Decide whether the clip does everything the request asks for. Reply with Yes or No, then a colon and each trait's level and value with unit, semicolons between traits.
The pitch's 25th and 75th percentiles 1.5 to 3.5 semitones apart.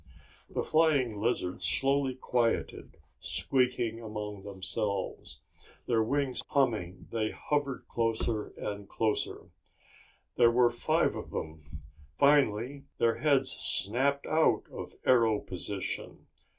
No: average, 4.4 semitones